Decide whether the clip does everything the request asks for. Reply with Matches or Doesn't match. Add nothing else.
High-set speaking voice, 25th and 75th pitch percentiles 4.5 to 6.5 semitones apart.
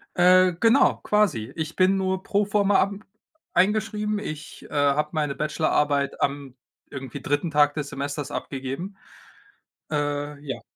Doesn't match